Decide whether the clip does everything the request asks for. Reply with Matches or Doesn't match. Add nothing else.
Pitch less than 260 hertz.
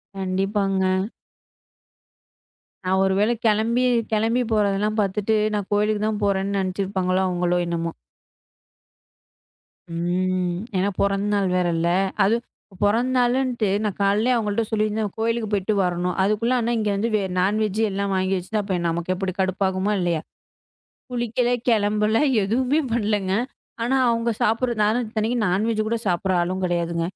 Matches